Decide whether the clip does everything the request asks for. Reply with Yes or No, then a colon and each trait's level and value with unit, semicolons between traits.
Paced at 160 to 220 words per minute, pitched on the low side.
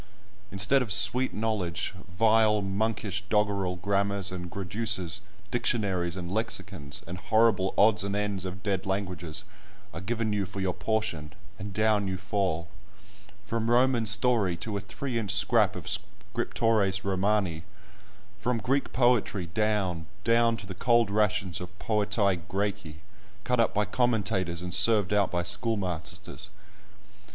No: slow, 135 wpm; low, 100 Hz